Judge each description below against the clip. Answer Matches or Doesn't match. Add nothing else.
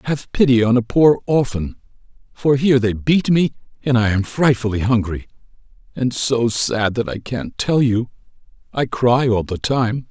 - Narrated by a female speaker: Doesn't match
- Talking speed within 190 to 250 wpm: Doesn't match